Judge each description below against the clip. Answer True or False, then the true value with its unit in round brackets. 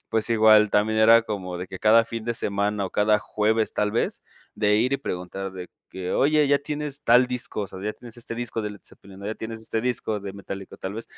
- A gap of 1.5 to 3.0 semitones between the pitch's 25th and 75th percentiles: True (2.5 semitones)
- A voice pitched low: True (110 Hz)